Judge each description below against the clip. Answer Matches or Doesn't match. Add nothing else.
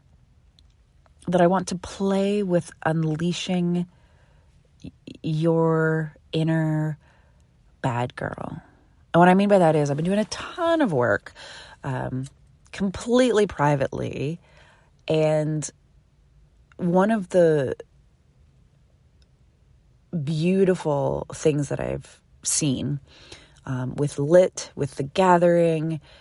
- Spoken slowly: Matches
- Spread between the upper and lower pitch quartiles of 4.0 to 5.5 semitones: Matches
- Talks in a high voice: Doesn't match